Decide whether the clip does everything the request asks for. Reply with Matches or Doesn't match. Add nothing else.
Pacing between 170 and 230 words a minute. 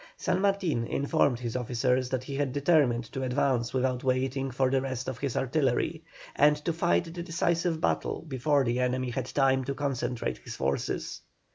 Matches